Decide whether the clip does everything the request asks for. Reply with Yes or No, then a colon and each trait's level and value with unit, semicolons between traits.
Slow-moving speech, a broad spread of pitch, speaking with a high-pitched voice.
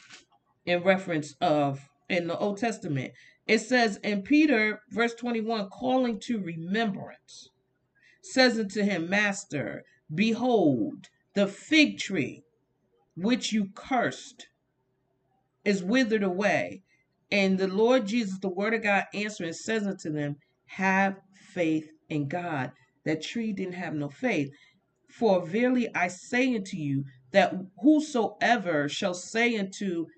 Yes: slow, 125 wpm; wide, 6.3 semitones; high, 195 Hz